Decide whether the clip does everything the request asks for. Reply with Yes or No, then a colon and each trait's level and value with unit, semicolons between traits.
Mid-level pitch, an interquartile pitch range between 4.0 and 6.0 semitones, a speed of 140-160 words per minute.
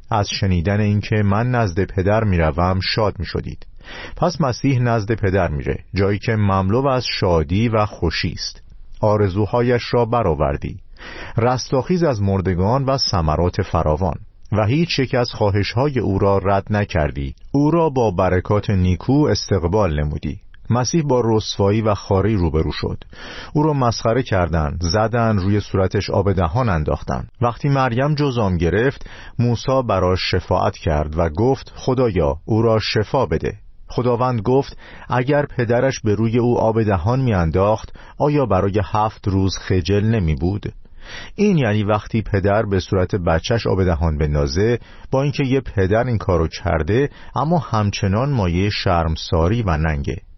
No: low, 105 Hz; average, 4.8 semitones; average, 145 wpm